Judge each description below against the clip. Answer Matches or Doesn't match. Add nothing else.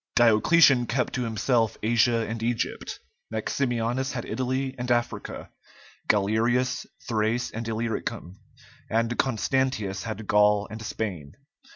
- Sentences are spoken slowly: Matches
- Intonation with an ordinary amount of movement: Doesn't match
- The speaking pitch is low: Matches